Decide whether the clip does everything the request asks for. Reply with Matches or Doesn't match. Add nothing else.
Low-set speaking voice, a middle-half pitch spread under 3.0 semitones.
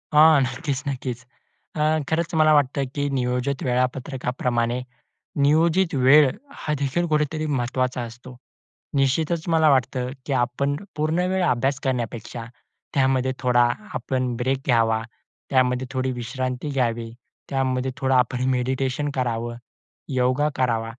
Matches